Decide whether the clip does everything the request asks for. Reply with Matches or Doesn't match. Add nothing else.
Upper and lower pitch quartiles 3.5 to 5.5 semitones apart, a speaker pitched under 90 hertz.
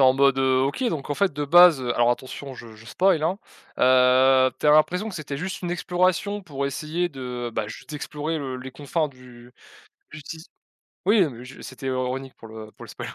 Doesn't match